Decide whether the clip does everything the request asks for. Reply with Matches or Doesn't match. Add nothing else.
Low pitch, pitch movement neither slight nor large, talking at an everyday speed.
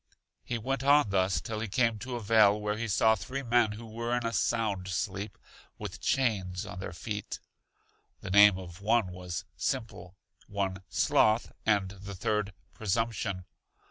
Matches